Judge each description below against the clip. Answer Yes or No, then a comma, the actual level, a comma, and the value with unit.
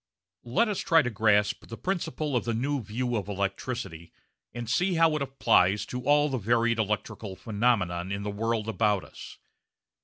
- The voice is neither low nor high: No, low, 115 Hz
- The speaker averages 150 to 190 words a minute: Yes, average, 175 wpm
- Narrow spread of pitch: No, average, 4.6 semitones